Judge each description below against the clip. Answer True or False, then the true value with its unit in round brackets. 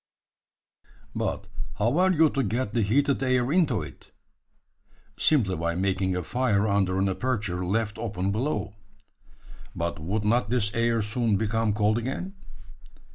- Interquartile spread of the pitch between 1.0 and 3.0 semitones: False (4.2 semitones)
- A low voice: True (110 Hz)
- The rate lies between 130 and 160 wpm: True (140 wpm)